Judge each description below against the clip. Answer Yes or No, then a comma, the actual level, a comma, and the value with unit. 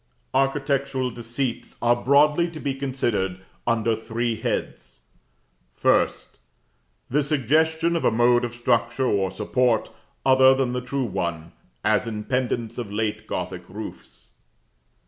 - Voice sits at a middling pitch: No, low, 120 Hz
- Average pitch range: Yes, average, 3.4 semitones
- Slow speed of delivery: Yes, slow, 125 wpm